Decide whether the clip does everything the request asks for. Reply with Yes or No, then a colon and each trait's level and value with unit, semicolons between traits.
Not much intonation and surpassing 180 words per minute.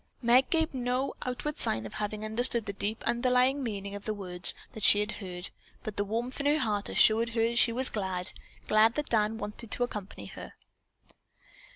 No: average, 3.4 semitones; average, 195 wpm